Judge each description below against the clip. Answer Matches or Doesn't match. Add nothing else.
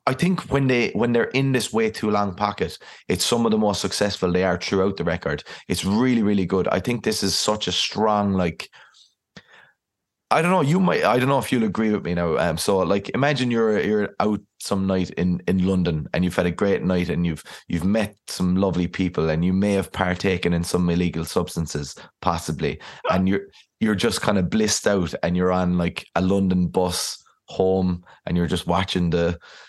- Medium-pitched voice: Doesn't match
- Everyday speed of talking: Doesn't match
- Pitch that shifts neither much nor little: Matches